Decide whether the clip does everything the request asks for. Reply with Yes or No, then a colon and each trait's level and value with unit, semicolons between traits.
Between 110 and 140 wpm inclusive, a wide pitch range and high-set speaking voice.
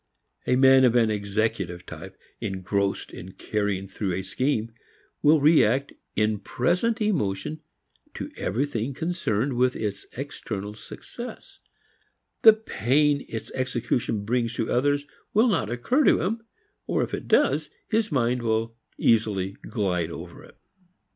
No: slow, 135 wpm; wide, 5.9 semitones; low, 120 Hz